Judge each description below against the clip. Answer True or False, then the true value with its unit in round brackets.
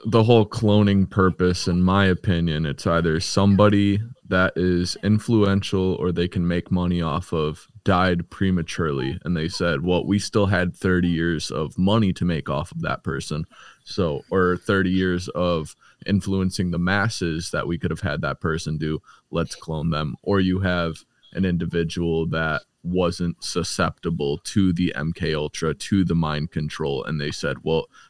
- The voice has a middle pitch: False (90 Hz)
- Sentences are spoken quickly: False (165 wpm)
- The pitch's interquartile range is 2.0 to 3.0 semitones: True (2.7 semitones)